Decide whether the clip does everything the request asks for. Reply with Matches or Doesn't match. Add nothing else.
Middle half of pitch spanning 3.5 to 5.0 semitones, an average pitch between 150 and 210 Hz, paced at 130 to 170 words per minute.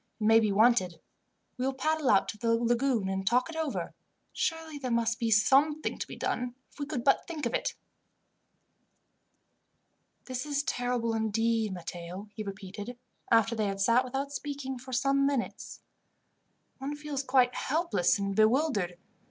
Doesn't match